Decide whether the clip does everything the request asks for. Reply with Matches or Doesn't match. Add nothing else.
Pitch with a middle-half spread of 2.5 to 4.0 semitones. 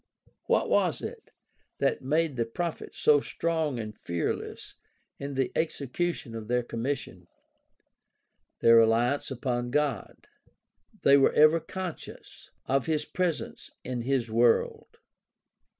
Doesn't match